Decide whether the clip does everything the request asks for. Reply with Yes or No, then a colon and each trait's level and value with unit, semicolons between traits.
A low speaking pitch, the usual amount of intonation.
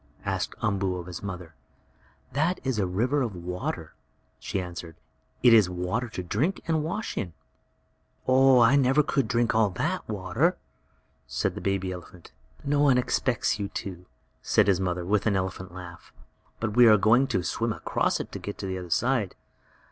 No: low, 105 Hz; wide, 5.7 semitones